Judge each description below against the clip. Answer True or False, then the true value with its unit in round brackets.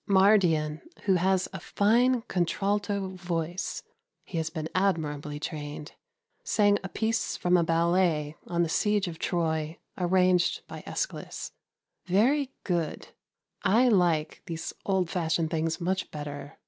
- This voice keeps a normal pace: False (130 wpm)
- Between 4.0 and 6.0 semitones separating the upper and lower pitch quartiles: False (3.5 semitones)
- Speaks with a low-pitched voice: False (175 Hz)